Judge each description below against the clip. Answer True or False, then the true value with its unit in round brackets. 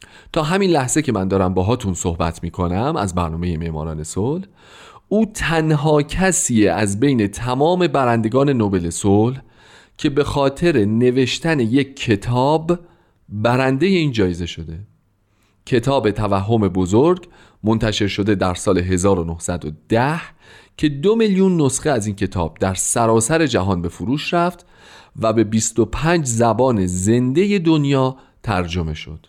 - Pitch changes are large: True (7.3 semitones)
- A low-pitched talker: True (115 Hz)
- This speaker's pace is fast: False (125 wpm)